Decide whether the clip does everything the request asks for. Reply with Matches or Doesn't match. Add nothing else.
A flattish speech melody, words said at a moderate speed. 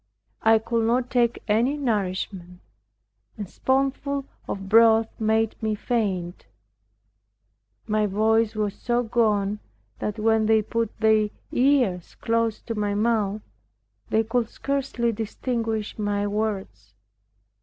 Doesn't match